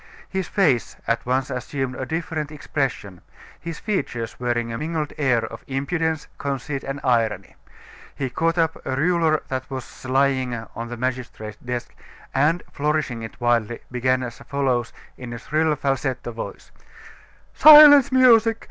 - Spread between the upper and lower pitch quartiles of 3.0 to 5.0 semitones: Yes, average, 4.4 semitones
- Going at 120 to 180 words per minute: Yes, average, 145 wpm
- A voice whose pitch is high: No, low, 135 Hz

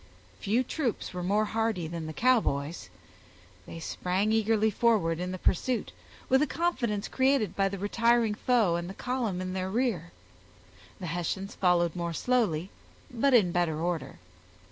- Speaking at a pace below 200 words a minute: Yes, average, 155 wpm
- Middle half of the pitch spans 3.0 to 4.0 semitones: No, average, 5.0 semitones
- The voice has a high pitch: Yes, high, 200 Hz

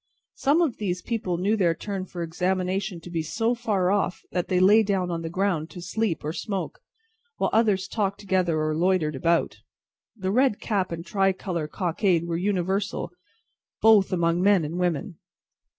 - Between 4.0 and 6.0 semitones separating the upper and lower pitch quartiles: No, average, 3.0 semitones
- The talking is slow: No, average, 175 wpm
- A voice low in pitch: No, medium, 185 Hz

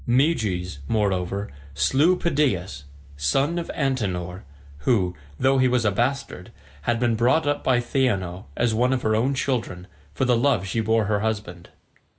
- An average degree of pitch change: No, wide, 5.8 semitones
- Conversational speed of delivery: Yes, average, 160 wpm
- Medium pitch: No, low, 115 Hz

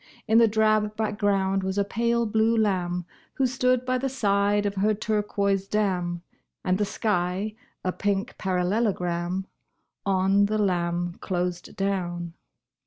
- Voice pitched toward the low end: No, high, 200 Hz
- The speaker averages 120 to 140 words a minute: Yes, slow, 135 wpm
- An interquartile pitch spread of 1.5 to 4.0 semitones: Yes, average, 2.8 semitones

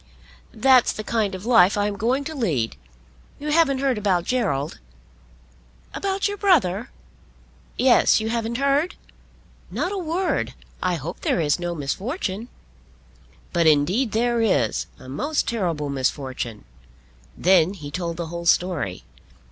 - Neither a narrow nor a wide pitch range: No, wide, 7.6 semitones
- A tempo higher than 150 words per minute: No, slow, 135 wpm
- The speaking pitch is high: Yes, high, 205 Hz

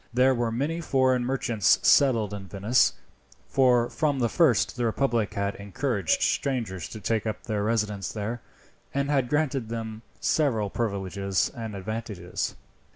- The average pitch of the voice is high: No, low, 115 Hz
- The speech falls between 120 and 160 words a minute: Yes, average, 145 wpm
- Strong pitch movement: No, average, 4.0 semitones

